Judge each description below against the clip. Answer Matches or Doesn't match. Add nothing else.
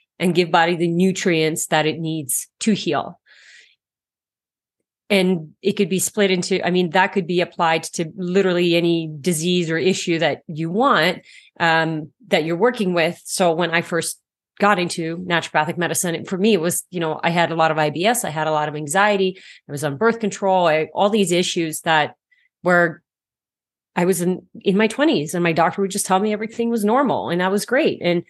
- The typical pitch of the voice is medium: Matches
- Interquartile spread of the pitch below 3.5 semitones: Matches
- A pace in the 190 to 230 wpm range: Matches